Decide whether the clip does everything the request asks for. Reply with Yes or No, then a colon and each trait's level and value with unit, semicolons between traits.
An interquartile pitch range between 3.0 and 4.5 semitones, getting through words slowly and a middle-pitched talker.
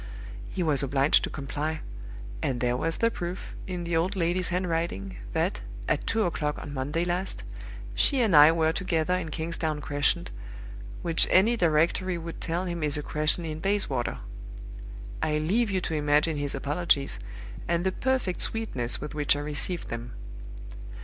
No: average, 3.4 semitones; average, 165 wpm; medium, 165 Hz